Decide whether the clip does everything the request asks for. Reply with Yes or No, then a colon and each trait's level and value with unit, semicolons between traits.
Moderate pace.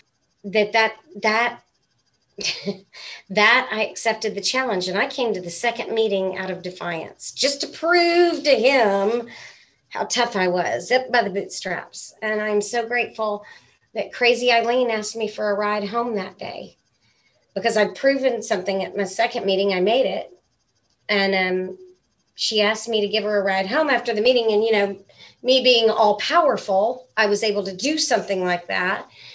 Yes: average, 175 wpm